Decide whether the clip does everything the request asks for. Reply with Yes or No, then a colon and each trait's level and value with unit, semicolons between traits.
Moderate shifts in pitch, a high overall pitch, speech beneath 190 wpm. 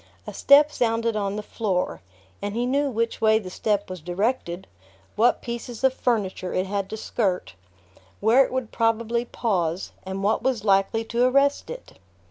Yes: average, 3.7 semitones; high, 225 Hz; average, 170 wpm